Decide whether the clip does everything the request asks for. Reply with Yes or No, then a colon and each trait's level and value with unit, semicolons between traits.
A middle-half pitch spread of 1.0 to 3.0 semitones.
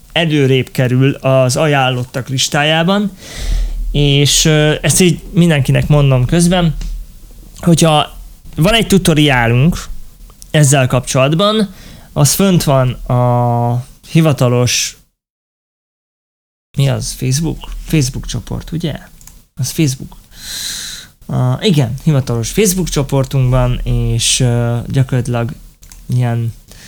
No: average, 4.4 semitones